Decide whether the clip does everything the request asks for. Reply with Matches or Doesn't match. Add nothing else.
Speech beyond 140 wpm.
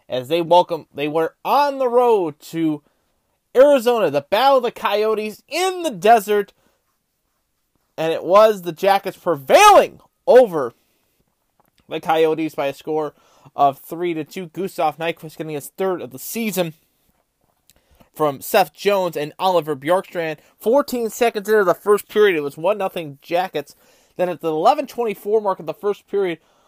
Matches